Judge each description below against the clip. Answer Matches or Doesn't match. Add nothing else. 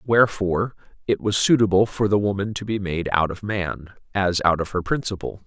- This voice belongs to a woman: Doesn't match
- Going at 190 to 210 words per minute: Matches